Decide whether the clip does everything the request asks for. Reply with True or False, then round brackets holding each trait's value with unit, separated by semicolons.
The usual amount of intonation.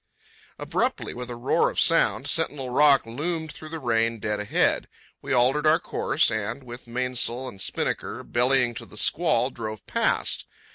True (3.3 semitones)